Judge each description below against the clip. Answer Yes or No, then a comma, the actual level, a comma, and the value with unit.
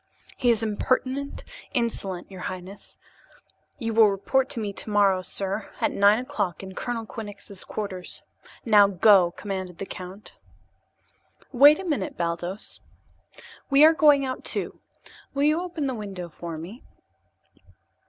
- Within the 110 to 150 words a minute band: Yes, slow, 135 wpm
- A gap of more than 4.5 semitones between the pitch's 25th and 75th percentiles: Yes, average, 5.1 semitones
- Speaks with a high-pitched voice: Yes, high, 205 Hz